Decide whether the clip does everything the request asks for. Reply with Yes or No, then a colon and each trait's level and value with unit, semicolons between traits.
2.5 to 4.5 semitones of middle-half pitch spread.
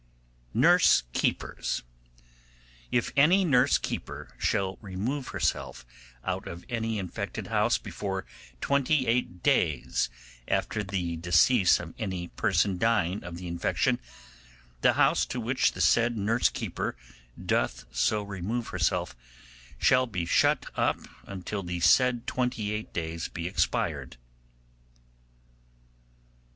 No: wide, 5.6 semitones